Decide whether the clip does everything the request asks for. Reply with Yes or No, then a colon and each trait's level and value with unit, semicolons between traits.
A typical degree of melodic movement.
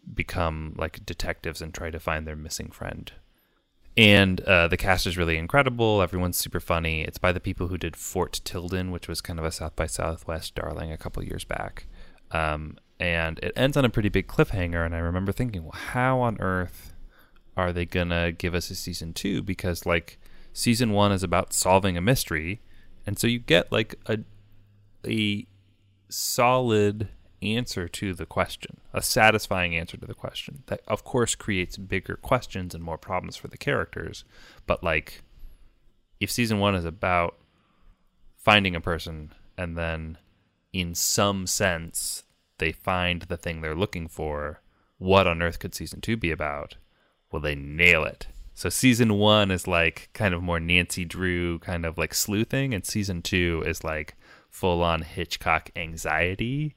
Yes: average, 3.5 semitones